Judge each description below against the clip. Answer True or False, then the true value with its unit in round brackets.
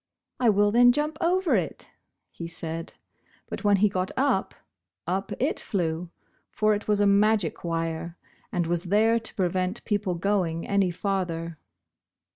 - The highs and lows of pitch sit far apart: False (3.9 semitones)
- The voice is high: True (195 Hz)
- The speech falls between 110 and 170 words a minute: True (150 wpm)